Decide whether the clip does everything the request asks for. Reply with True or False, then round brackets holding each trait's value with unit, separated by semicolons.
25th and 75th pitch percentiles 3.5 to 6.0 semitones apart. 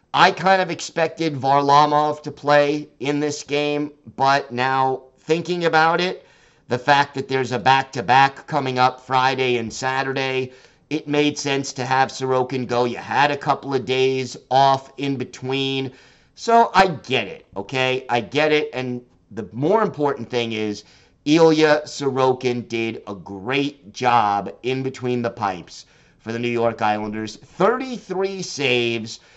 False (3.0 semitones)